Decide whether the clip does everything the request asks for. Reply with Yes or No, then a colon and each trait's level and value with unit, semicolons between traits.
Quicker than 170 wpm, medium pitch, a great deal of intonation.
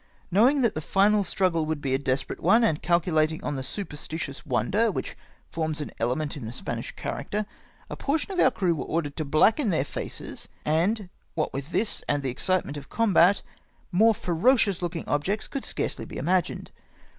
Yes: average, 185 wpm; medium, 170 Hz; wide, 5.8 semitones